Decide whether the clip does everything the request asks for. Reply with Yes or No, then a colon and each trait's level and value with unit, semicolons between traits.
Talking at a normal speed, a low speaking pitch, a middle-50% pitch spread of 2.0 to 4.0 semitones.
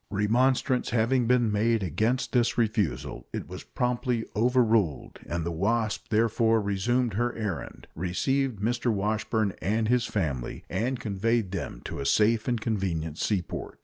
Yes: average, 145 wpm; low, 110 Hz; average, 3.4 semitones